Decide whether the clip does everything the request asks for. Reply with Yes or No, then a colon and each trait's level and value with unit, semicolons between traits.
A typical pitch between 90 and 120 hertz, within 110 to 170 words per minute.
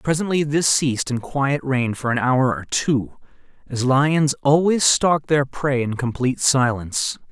No: low, 135 Hz; average, 165 wpm